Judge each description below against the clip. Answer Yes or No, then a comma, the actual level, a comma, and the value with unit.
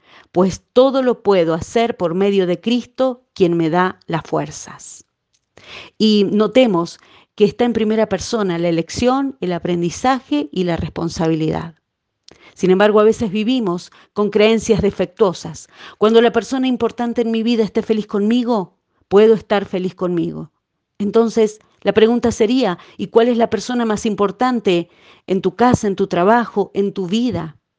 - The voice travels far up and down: No, average, 4.0 semitones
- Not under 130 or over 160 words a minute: Yes, average, 150 wpm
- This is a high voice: Yes, high, 215 Hz